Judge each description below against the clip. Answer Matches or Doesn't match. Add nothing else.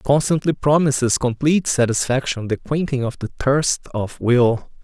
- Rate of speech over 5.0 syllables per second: Doesn't match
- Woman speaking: Doesn't match